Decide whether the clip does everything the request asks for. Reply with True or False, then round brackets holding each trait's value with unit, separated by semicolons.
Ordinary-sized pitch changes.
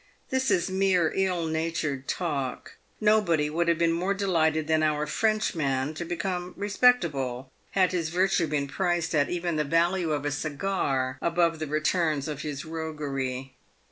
True (3.2 semitones)